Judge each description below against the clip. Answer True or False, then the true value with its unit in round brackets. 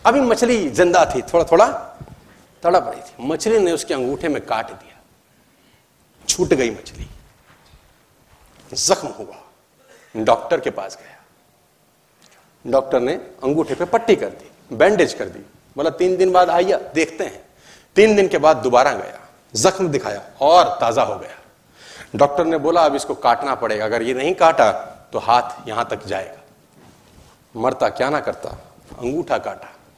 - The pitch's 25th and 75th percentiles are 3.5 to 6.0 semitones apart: True (4.4 semitones)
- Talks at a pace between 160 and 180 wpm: False (150 wpm)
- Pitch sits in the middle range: True (180 Hz)